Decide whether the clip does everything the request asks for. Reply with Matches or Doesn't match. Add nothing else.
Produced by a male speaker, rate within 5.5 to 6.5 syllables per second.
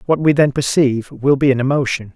Matches